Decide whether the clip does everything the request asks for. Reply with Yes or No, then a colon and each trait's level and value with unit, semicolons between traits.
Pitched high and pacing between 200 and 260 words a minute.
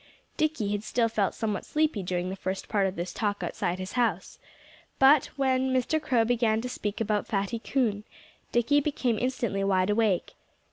No: high, 220 Hz; average, 175 wpm